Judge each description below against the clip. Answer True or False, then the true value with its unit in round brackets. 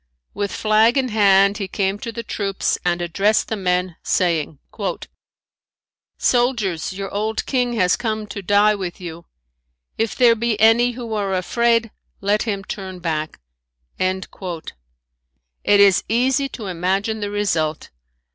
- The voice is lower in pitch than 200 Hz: False (205 Hz)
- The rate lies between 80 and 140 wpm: True (135 wpm)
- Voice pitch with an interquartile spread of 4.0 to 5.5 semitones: False (3.2 semitones)